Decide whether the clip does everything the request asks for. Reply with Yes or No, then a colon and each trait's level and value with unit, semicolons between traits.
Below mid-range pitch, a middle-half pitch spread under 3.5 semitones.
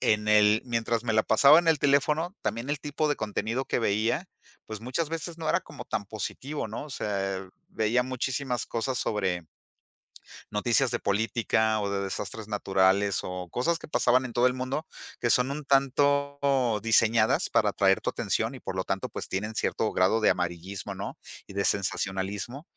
No: low, 115 Hz; average, 4.9 semitones